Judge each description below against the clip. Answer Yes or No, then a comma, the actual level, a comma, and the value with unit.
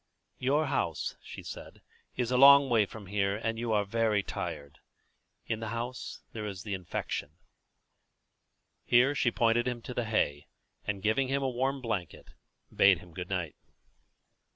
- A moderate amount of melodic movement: Yes, average, 4.1 semitones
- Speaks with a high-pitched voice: No, low, 115 Hz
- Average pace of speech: Yes, average, 165 wpm